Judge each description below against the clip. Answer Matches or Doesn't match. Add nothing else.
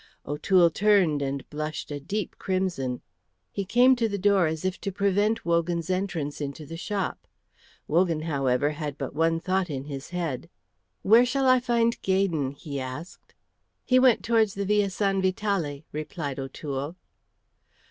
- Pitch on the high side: Doesn't match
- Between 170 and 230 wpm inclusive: Doesn't match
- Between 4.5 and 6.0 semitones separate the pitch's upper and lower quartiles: Matches